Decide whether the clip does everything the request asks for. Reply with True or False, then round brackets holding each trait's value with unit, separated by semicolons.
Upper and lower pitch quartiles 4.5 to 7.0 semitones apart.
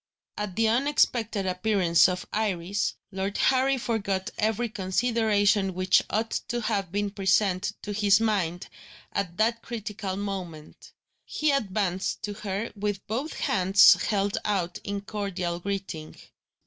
False (2.6 semitones)